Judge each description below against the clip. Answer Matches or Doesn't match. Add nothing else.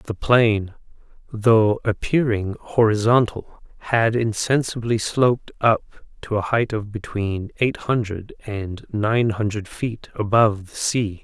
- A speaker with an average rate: Doesn't match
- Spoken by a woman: Doesn't match